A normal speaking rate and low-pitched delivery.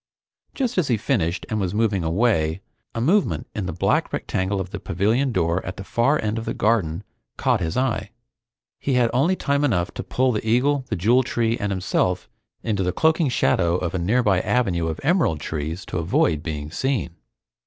Yes: average, 195 wpm; low, 105 Hz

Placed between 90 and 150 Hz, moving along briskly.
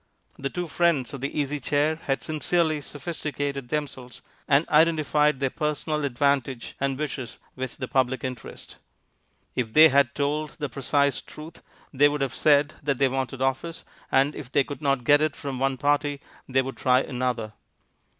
No: medium, 140 Hz; average, 170 wpm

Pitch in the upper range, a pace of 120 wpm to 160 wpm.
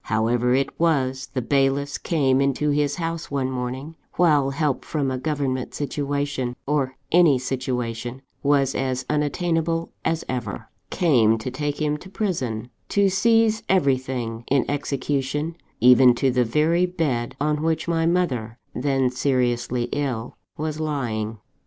No: medium, 140 Hz; average, 140 wpm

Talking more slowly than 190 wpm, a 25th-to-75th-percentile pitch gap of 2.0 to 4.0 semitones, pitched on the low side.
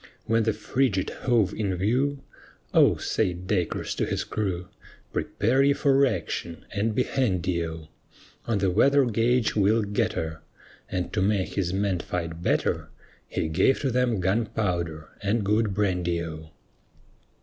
No: average, 150 wpm; average, 4.4 semitones; low, 100 Hz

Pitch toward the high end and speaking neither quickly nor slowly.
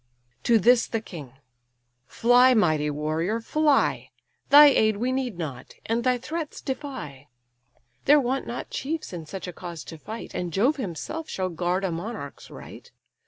Yes: high, 220 Hz; average, 160 wpm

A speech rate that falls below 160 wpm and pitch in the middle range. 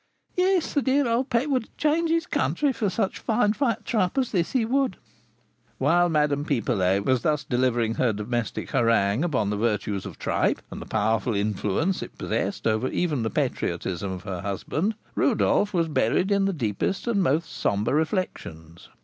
No: average, 175 wpm; medium, 150 Hz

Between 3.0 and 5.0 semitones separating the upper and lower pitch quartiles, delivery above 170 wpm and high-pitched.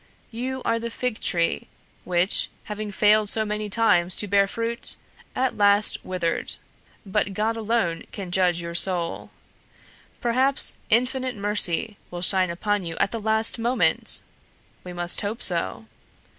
No: average, 4.1 semitones; average, 145 wpm; high, 205 Hz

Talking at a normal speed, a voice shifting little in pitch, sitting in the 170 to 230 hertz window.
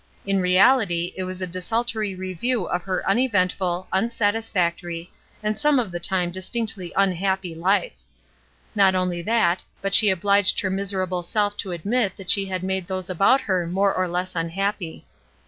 Yes: average, 160 wpm; narrow, 2.1 semitones; high, 190 Hz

